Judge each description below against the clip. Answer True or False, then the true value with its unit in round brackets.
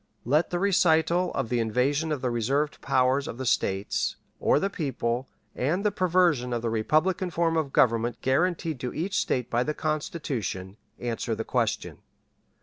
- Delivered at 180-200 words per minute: False (165 wpm)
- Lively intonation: True (5.7 semitones)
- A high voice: False (140 Hz)